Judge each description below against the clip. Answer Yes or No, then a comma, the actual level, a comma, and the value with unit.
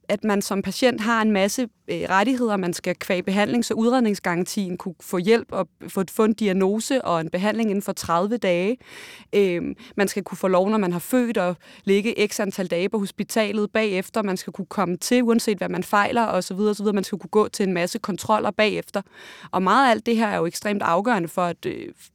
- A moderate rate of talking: No, fast, 230 wpm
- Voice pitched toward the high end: Yes, high, 205 Hz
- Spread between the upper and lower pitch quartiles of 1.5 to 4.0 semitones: Yes, average, 2.9 semitones